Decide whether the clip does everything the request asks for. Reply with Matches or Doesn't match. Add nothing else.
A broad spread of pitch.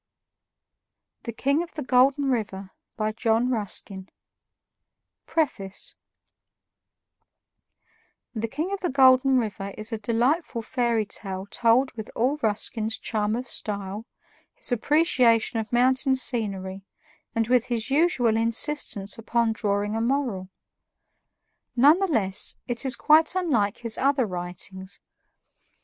Doesn't match